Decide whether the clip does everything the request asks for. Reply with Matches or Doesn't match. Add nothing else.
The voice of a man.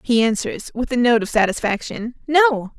Doesn't match